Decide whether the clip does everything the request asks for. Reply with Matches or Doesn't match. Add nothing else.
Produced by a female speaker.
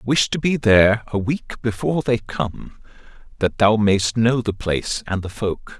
Doesn't match